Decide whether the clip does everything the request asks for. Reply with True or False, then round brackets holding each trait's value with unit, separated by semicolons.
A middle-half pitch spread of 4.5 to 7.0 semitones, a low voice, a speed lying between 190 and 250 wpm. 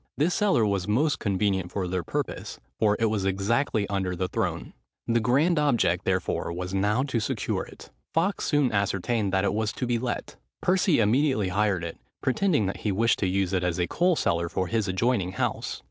True (5.0 semitones; 105 Hz; 195 wpm)